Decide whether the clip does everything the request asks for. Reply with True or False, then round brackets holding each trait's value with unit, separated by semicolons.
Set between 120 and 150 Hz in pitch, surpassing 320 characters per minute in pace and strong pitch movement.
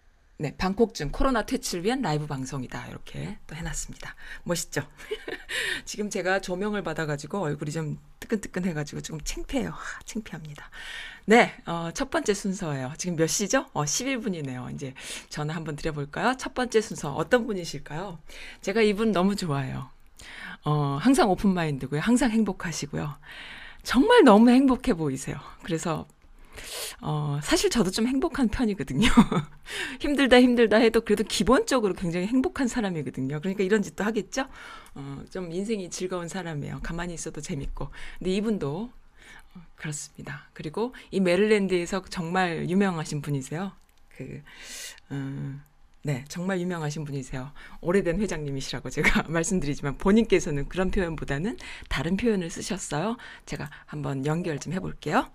False (185 Hz; 345 characters per minute; 6.6 semitones)